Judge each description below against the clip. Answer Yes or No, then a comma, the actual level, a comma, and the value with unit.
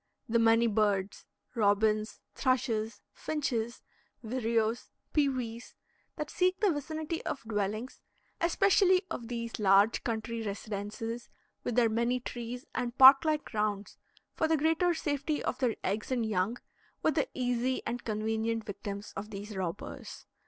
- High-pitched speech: Yes, high, 230 Hz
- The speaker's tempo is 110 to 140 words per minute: Yes, slow, 135 wpm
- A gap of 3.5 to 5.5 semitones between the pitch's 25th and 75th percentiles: Yes, average, 3.8 semitones